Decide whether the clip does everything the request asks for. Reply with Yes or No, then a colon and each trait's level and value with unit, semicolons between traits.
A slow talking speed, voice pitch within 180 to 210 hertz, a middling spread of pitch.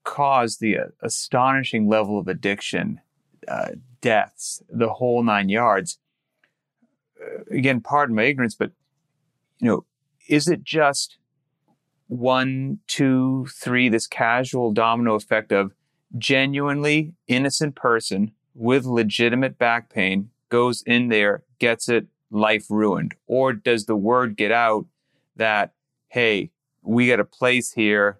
No: slow, 125 wpm; low, 120 Hz; average, 3.9 semitones